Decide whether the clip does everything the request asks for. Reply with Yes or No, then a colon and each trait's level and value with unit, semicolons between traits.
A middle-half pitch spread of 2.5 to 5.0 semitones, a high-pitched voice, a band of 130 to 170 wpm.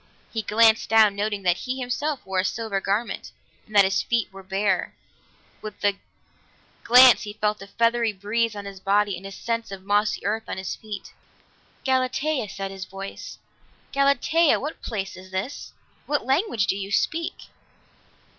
Yes: average, 3.6 semitones; high, 210 Hz; average, 165 wpm